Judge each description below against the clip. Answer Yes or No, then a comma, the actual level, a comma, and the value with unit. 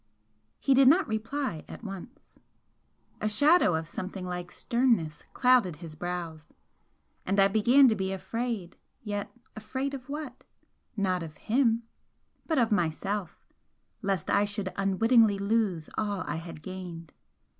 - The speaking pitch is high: Yes, high, 200 Hz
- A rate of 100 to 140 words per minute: Yes, slow, 135 wpm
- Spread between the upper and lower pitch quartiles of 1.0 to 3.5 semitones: No, average, 5.0 semitones